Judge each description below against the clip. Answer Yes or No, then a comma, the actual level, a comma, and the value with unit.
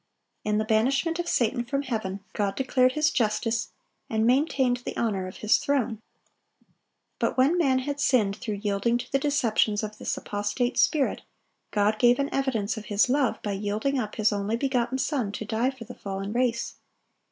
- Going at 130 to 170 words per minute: No, average, 185 wpm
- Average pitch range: Yes, average, 4.0 semitones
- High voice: Yes, high, 235 Hz